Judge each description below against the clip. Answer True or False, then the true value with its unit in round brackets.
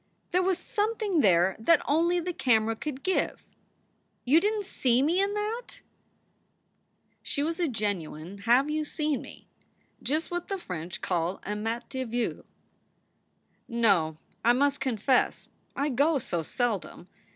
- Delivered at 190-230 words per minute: False (155 wpm)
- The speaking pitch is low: False (265 Hz)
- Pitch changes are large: True (7.6 semitones)